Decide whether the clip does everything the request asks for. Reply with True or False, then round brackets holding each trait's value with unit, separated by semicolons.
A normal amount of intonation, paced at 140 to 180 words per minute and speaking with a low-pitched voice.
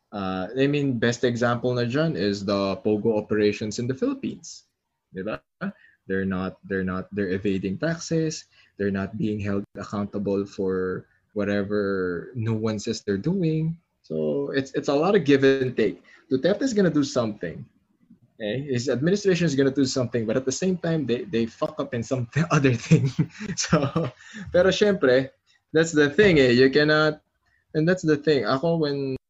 False (7.0 semitones; 170 wpm; 130 Hz)